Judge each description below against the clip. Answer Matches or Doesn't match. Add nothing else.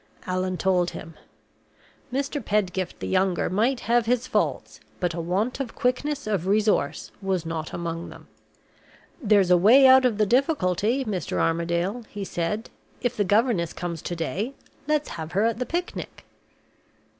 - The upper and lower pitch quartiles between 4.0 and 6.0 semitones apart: Matches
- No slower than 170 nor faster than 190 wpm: Doesn't match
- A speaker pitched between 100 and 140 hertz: Doesn't match